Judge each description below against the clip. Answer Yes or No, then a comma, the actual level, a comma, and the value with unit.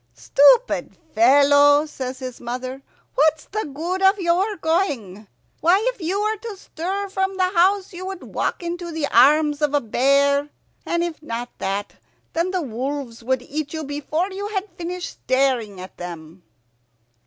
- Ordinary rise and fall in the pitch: No, wide, 6.1 semitones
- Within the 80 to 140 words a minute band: No, average, 160 wpm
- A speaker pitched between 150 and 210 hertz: No, very high, 305 Hz